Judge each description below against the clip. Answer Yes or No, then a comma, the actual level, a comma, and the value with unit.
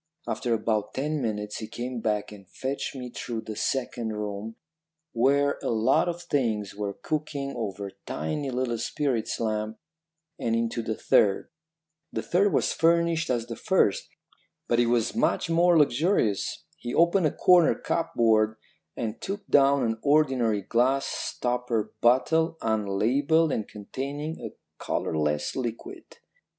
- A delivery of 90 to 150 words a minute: Yes, average, 140 wpm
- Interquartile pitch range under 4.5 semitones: No, average, 5.0 semitones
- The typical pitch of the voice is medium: No, low, 120 Hz